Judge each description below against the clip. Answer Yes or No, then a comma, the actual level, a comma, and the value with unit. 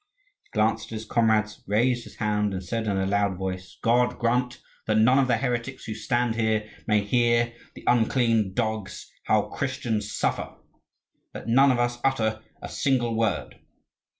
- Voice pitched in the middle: No, low, 115 Hz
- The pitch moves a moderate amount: No, narrow, 2.2 semitones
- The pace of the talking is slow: No, average, 170 wpm